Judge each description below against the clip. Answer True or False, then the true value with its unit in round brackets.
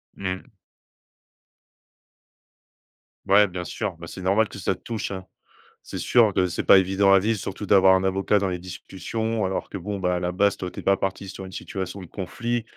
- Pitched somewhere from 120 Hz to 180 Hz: False (95 Hz)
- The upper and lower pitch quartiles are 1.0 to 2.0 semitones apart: True (1.7 semitones)